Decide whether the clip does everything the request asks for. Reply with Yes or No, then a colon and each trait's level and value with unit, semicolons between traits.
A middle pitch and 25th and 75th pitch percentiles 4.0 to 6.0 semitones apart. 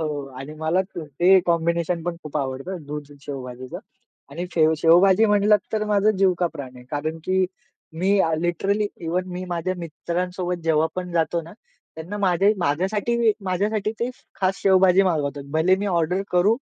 No: medium, 175 Hz; average, 3.3 semitones